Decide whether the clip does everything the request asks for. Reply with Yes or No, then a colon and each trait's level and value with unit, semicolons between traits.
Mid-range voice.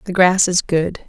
Yes: medium, 180 Hz